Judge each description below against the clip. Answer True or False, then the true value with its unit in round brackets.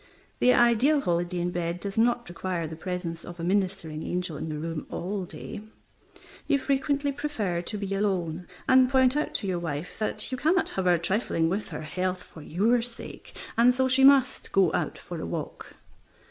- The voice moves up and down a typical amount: False (6.1 semitones)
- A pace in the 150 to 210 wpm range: True (190 wpm)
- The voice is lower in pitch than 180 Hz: False (190 Hz)